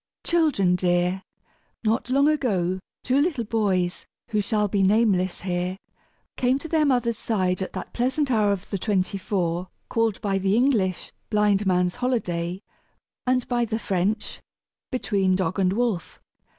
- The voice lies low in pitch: No, high, 205 Hz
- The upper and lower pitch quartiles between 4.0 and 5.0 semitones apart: Yes, average, 4.6 semitones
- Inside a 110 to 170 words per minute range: Yes, average, 150 wpm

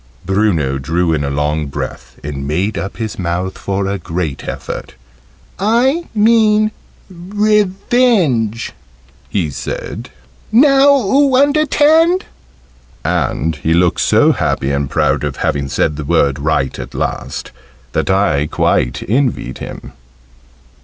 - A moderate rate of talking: No, slow, 125 wpm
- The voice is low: Yes, low, 100 Hz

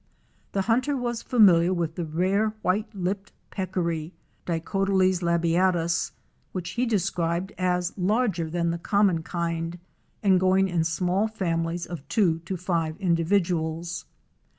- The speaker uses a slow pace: Yes, slow, 130 wpm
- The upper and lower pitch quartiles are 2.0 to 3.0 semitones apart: Yes, narrow, 2.6 semitones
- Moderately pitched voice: Yes, medium, 180 Hz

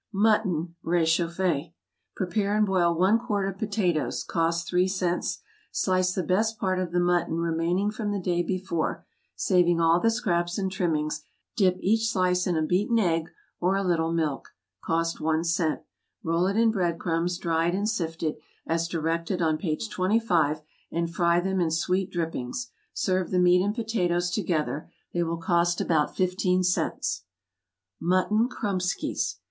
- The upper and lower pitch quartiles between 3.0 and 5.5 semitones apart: No, narrow, 2.4 semitones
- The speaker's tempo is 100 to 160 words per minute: Yes, average, 155 wpm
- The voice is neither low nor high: Yes, medium, 180 Hz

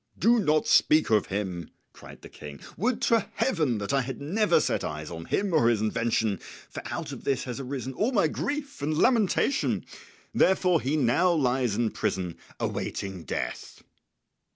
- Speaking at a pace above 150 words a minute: Yes, average, 170 wpm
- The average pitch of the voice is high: No, low, 135 Hz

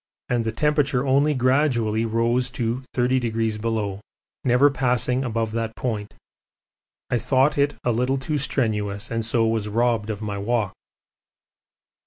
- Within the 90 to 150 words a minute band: Yes, slow, 135 wpm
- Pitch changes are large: No, average, 2.7 semitones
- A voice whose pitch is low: Yes, low, 120 Hz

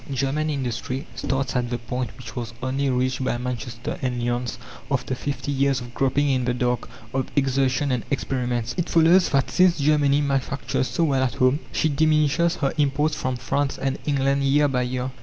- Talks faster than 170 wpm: Yes, average, 185 wpm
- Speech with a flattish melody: Yes, narrow, 2.3 semitones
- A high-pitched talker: No, low, 135 Hz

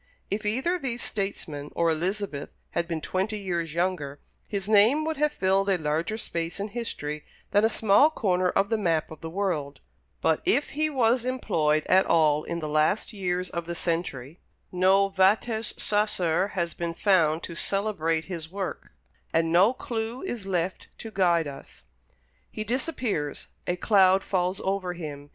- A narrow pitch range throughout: No, average, 4.5 semitones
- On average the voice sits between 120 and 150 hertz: No, medium, 185 Hz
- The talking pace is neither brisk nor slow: Yes, average, 165 wpm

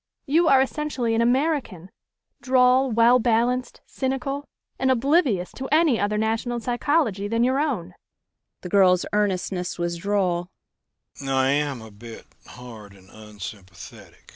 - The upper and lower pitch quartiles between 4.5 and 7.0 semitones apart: Yes, average, 4.8 semitones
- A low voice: No, high, 240 Hz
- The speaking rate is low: Yes, slow, 100 wpm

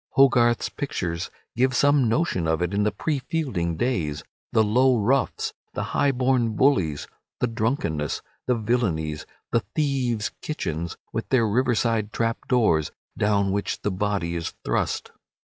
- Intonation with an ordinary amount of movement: No, wide, 5.9 semitones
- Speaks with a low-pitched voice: Yes, low, 110 Hz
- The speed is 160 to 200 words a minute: No, average, 140 wpm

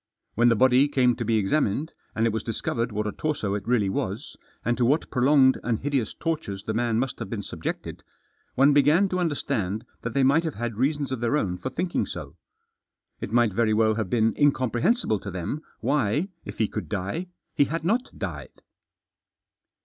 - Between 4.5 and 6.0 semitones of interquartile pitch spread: Yes, average, 4.9 semitones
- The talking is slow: No, average, 190 wpm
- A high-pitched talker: No, low, 120 Hz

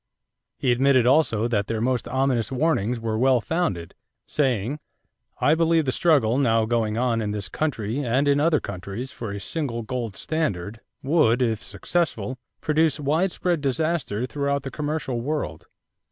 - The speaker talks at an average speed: Yes, average, 155 wpm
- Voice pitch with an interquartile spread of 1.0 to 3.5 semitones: No, average, 4.9 semitones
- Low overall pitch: Yes, low, 130 Hz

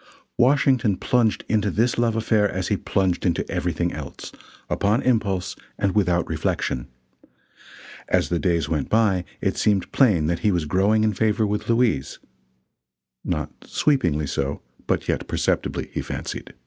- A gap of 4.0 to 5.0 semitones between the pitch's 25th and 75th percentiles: Yes, average, 4.4 semitones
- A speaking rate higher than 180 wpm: No, average, 150 wpm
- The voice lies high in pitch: No, low, 100 Hz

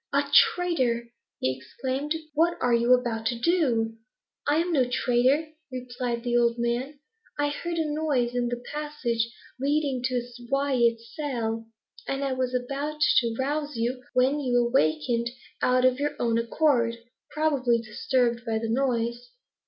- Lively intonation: No, average, 3.3 semitones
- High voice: Yes, very high, 250 Hz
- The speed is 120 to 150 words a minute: Yes, average, 145 wpm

